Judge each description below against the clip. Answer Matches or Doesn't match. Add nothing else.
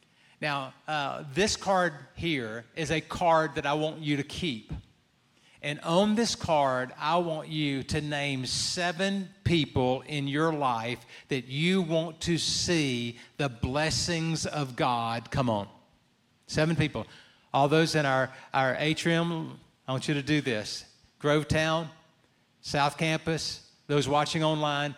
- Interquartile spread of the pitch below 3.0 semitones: Doesn't match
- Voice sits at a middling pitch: Matches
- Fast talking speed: Doesn't match